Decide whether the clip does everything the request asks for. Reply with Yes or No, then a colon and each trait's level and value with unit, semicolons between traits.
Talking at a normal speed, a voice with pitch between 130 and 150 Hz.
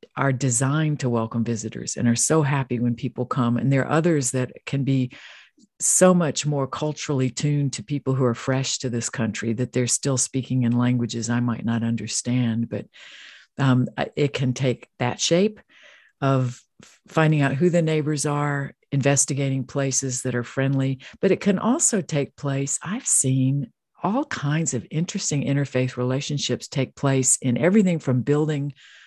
Yes: average, 165 wpm; low, 135 Hz